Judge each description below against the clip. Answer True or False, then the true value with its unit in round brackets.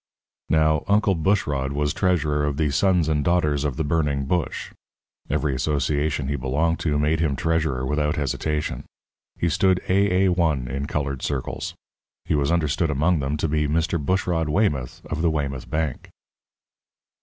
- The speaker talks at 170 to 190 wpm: False (155 wpm)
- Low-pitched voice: True (75 Hz)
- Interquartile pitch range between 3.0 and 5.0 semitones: False (2.6 semitones)